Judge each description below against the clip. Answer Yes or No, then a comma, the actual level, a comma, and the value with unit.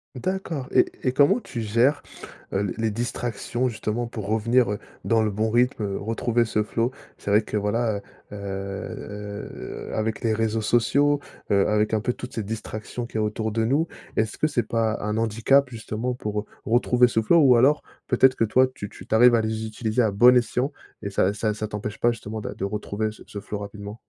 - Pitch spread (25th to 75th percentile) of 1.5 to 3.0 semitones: Yes, narrow, 2.5 semitones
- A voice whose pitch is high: No, low, 110 Hz